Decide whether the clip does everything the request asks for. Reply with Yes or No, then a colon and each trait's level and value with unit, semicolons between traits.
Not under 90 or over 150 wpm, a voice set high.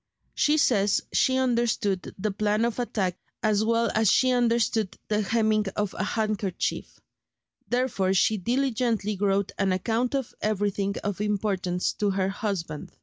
Yes: average, 145 wpm; high, 210 Hz